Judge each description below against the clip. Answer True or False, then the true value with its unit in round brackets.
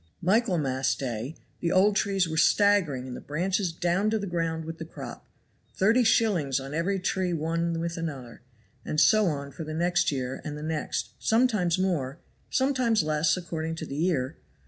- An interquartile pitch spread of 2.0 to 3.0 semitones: False (4.2 semitones)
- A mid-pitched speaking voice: True (165 Hz)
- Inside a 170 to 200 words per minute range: True (175 wpm)